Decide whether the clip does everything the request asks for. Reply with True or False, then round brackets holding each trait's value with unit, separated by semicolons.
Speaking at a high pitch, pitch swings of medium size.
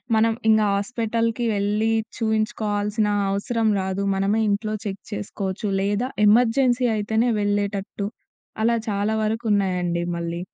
False (210 Hz; 2.0 semitones)